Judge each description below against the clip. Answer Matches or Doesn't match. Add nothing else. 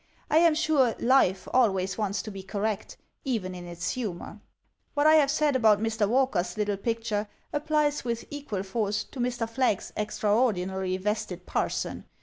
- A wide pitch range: Doesn't match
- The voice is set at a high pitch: Matches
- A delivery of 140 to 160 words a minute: Matches